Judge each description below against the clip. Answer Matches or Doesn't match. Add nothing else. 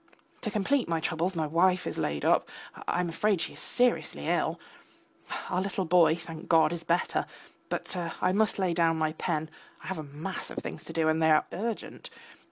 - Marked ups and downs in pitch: Doesn't match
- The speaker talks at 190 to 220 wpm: Matches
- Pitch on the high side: Doesn't match